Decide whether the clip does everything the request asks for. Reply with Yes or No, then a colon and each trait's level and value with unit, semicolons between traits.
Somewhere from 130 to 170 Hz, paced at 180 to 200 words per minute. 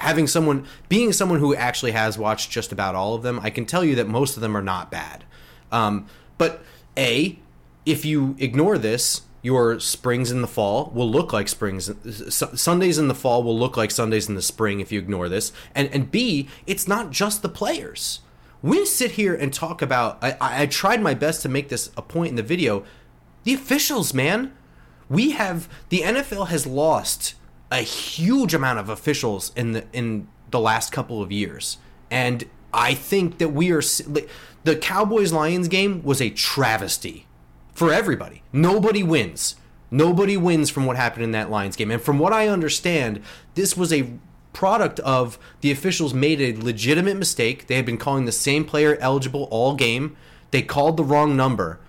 Yes: low, 135 Hz; average, 185 wpm